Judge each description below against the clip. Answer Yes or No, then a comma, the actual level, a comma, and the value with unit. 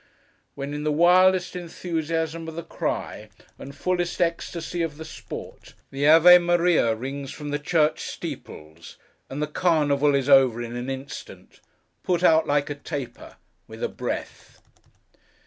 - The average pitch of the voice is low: No, medium, 150 Hz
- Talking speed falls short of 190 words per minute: Yes, average, 145 wpm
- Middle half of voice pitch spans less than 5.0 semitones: Yes, average, 3.5 semitones